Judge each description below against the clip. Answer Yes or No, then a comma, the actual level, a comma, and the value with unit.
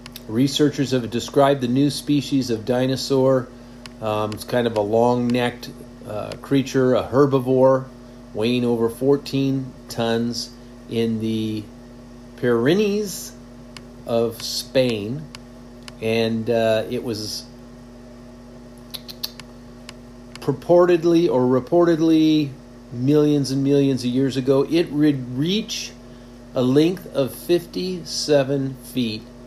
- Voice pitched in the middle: No, low, 125 Hz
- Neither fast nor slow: No, slow, 100 wpm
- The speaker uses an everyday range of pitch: No, narrow, 2.0 semitones